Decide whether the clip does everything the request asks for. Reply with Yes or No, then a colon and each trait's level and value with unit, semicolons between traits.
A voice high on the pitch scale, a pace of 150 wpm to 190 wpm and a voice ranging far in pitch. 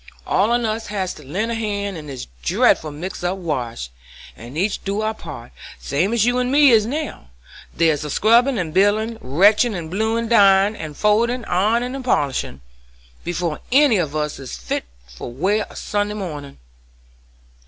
Yes: high, 200 Hz; average, 170 wpm; wide, 6.6 semitones